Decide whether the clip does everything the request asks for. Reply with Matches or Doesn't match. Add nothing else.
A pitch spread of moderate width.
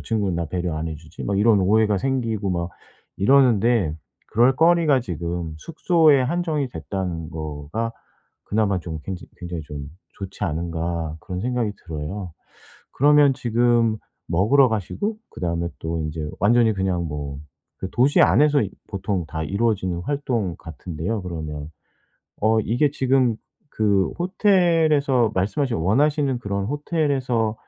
Doesn't match